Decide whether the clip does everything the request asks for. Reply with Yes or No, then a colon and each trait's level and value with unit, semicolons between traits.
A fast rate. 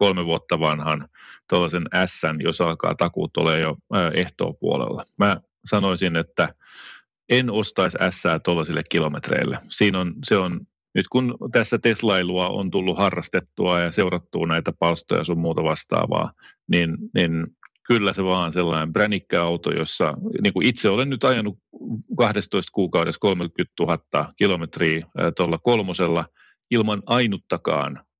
No: average, 130 wpm